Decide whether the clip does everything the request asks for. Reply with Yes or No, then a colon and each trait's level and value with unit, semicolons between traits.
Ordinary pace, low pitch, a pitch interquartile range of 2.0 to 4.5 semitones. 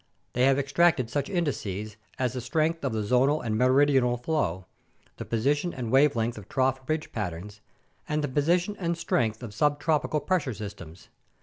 No: average, 165 wpm; low, 130 Hz; average, 5.1 semitones